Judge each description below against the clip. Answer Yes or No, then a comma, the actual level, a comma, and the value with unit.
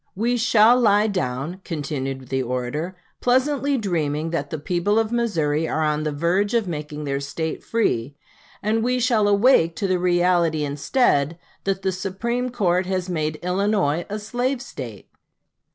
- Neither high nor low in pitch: Yes, medium, 180 Hz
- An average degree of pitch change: No, wide, 6.3 semitones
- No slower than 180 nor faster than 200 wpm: No, average, 155 wpm